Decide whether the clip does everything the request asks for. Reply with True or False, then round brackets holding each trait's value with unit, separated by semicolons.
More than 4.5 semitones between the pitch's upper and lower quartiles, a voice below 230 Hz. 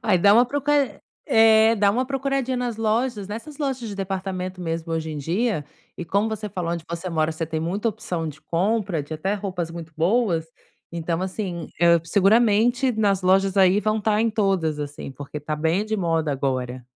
True (5.1 semitones; 190 Hz)